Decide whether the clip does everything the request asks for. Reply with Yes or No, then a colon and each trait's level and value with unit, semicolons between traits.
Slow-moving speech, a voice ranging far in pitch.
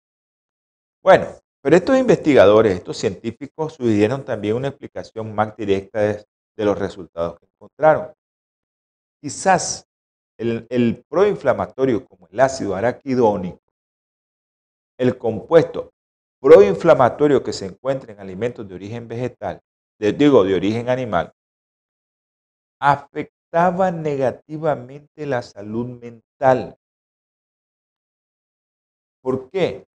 Yes: slow, 100 wpm; wide, 6.1 semitones